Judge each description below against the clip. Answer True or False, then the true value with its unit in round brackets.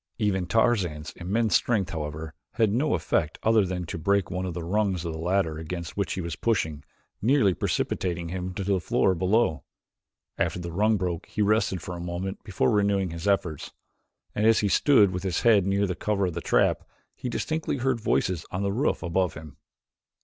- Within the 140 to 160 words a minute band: False (195 wpm)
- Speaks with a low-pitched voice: True (95 Hz)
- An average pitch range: True (3.5 semitones)